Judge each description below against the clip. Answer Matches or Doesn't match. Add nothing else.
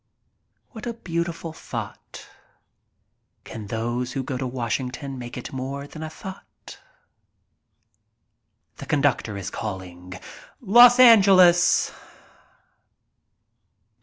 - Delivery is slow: Matches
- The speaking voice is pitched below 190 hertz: Matches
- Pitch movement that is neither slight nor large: Doesn't match